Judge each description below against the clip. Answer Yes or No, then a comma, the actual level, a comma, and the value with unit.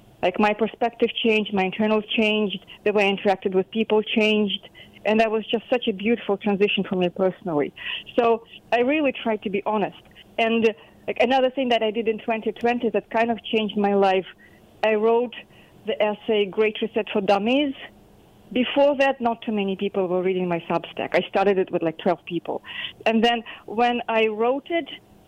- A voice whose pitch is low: No, high, 215 Hz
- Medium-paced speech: Yes, average, 185 wpm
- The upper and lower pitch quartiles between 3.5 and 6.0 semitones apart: No, average, 2.8 semitones